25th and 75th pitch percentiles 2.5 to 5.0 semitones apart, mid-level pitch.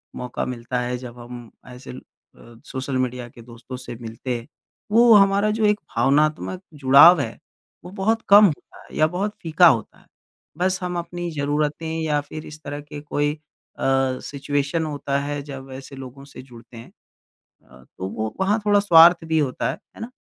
No: wide, 5.6 semitones; medium, 145 Hz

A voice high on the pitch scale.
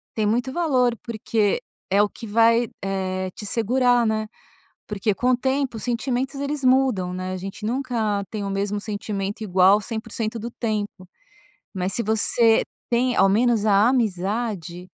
Yes: high, 220 Hz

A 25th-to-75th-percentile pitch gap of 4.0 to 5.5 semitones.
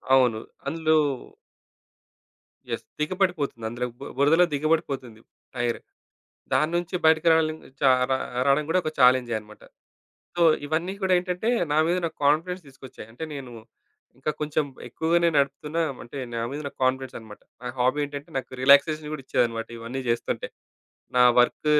Yes: average, 4.3 semitones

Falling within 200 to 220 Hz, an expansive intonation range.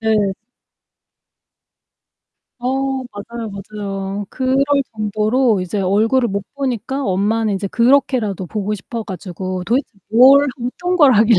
No: high, 215 Hz; average, 4.0 semitones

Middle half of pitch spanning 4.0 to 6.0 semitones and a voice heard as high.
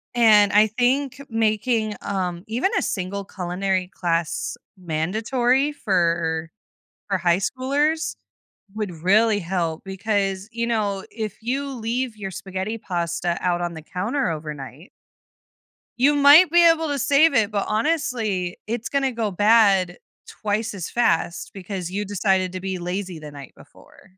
Yes: average, 4.7 semitones; high, 205 Hz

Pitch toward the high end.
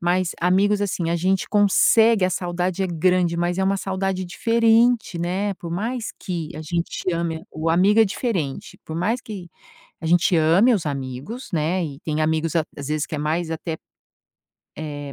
No: medium, 175 Hz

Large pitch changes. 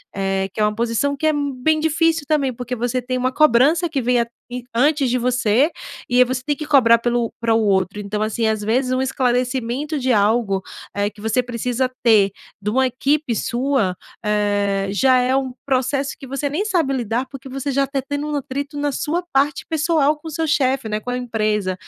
No: average, 3.9 semitones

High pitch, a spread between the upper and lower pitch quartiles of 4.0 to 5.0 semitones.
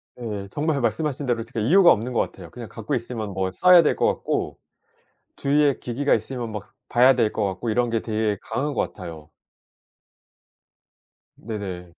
No: low, 115 Hz; average, 4.3 semitones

